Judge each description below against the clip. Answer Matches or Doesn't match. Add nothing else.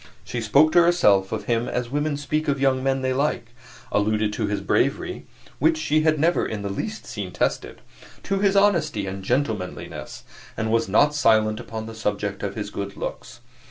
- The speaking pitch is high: Doesn't match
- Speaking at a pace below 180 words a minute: Doesn't match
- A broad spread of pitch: Matches